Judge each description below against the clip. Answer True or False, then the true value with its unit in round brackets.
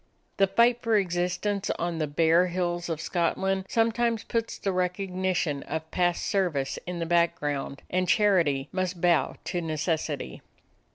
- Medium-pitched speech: True (175 Hz)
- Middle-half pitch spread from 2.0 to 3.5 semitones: True (2.9 semitones)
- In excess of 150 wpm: False (140 wpm)